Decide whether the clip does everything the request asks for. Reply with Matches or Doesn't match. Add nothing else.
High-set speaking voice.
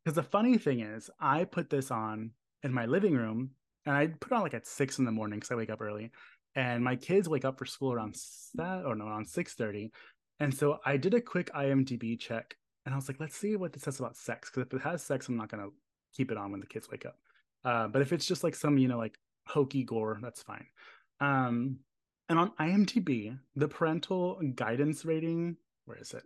Doesn't match